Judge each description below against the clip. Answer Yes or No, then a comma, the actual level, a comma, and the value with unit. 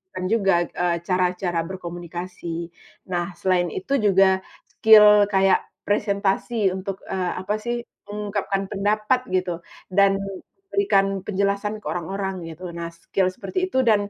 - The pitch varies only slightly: Yes, narrow, 2.2 semitones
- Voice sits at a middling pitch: No, high, 195 Hz